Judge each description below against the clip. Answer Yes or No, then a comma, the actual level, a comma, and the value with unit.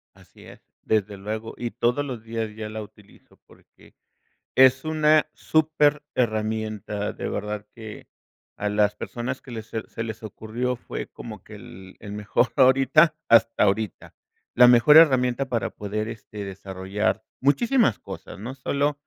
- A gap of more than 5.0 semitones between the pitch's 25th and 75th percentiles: No, average, 3.8 semitones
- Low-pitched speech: Yes, low, 115 Hz